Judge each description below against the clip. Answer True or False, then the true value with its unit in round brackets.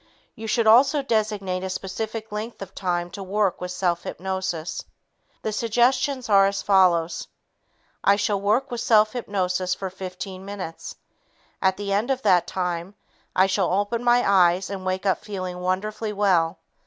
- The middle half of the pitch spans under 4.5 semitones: True (2.7 semitones)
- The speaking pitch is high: True (195 Hz)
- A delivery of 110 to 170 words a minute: True (160 wpm)